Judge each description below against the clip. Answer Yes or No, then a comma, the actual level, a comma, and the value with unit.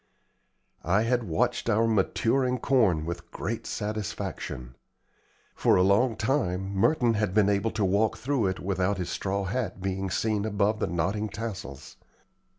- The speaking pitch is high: No, low, 100 Hz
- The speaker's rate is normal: Yes, average, 150 wpm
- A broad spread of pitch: No, average, 3.1 semitones